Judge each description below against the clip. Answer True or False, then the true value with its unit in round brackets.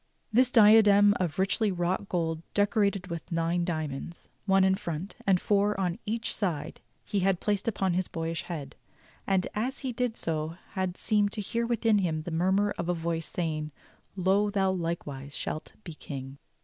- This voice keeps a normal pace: True (175 wpm)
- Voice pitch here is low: False (185 Hz)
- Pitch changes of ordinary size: True (3.8 semitones)